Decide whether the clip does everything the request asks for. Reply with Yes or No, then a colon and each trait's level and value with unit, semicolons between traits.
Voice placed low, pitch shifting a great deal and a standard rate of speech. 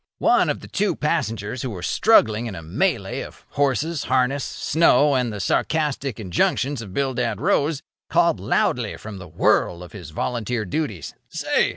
Yes: low, 125 Hz; wide, 5.8 semitones; average, 165 wpm